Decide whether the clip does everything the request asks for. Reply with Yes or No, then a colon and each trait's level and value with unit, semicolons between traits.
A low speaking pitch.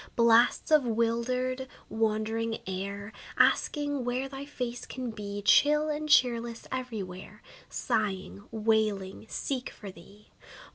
No: high, 230 Hz